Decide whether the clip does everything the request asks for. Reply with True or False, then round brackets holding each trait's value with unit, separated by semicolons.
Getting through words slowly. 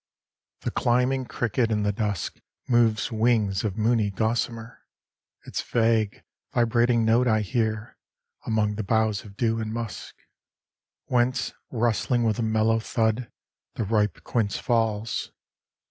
True (130 wpm)